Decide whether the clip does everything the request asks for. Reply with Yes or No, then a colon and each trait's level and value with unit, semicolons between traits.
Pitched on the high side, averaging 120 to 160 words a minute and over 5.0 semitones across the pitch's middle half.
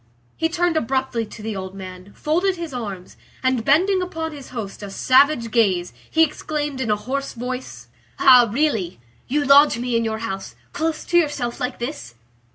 No: very high, 255 Hz; average, 175 wpm; wide, 5.5 semitones